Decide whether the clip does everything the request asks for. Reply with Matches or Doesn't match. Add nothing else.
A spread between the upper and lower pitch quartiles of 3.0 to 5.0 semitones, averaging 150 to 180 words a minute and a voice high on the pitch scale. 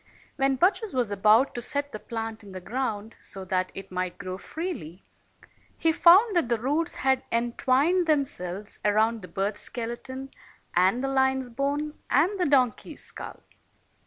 Doesn't match